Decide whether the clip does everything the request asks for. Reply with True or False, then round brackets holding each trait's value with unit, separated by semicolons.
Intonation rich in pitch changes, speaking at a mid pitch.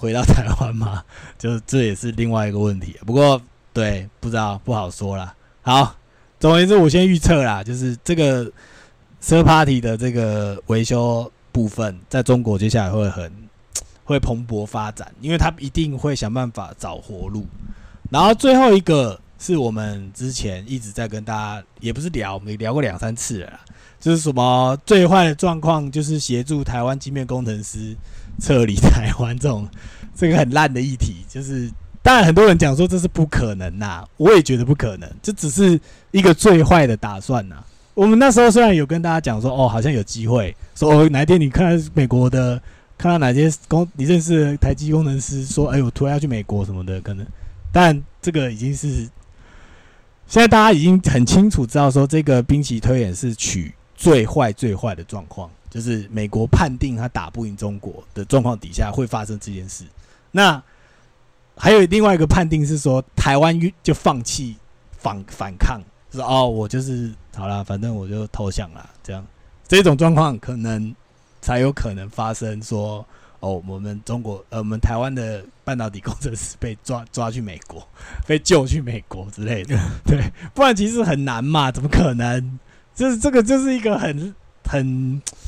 False (5.9 semitones; 120 Hz)